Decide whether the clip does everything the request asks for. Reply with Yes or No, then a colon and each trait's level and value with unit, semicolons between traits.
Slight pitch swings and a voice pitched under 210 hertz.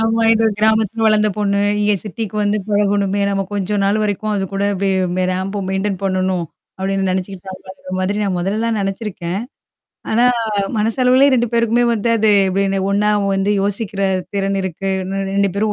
Yes: narrow, 1.9 semitones; high, 200 Hz